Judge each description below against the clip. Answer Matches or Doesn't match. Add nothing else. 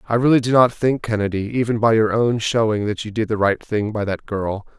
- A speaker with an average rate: Doesn't match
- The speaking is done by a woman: Doesn't match